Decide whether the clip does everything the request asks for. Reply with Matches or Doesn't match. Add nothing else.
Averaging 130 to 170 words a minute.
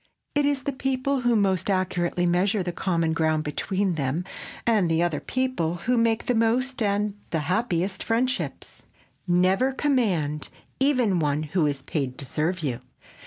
Matches